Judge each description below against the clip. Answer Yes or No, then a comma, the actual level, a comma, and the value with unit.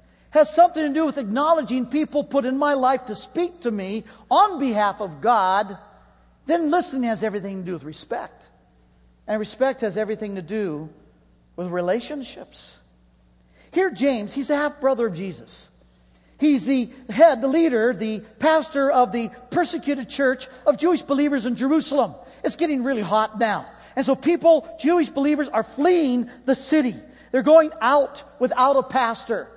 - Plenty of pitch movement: Yes, wide, 6.0 semitones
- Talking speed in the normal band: Yes, average, 160 wpm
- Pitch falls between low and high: No, very high, 255 Hz